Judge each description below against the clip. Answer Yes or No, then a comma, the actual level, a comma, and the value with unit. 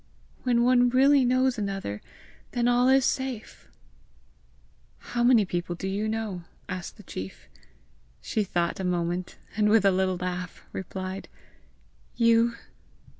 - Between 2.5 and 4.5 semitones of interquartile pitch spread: No, average, 5.0 semitones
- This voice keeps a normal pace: No, slow, 130 wpm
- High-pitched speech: Yes, high, 210 Hz